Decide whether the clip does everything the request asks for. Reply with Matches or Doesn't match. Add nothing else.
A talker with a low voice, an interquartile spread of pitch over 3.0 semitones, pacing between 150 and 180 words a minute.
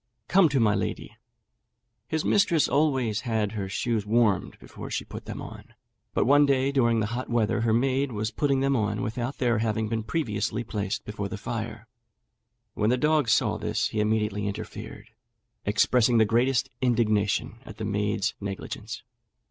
Matches